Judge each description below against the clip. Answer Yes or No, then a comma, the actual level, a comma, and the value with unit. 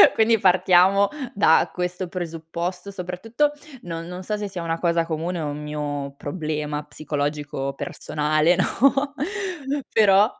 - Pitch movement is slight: No, average, 3.6 semitones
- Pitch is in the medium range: Yes, medium, 170 Hz